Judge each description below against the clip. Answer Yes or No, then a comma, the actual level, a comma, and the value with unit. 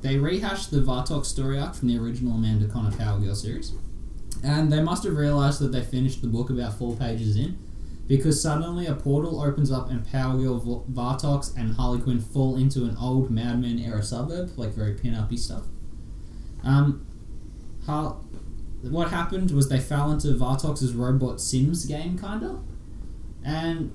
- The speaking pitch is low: Yes, low, 125 Hz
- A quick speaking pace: No, average, 175 wpm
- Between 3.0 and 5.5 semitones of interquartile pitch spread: Yes, average, 4.5 semitones